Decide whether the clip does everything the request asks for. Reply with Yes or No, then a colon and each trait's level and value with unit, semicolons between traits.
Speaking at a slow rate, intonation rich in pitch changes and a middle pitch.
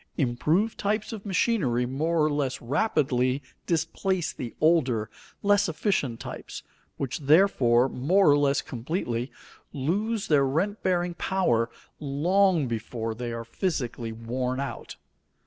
Yes: slow, 125 wpm; wide, 6.9 semitones; medium, 145 Hz